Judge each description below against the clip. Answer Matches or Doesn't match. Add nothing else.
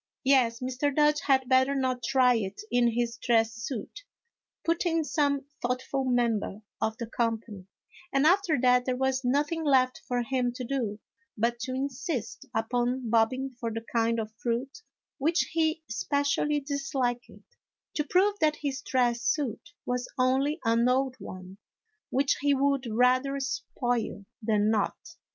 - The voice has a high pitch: Matches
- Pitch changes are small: Doesn't match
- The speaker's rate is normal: Matches